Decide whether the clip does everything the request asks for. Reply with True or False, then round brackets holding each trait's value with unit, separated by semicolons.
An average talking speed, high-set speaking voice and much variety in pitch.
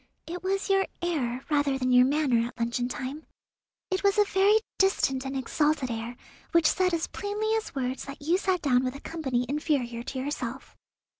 True (190 wpm; 285 Hz; 6.2 semitones)